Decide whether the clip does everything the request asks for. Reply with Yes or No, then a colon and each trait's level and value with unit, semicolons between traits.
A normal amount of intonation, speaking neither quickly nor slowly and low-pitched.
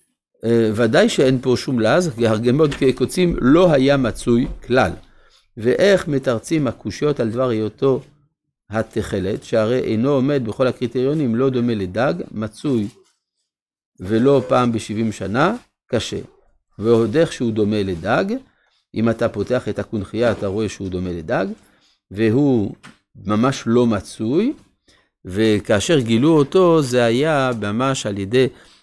Yes: average, 4.3 semitones; average, 125 wpm; low, 120 Hz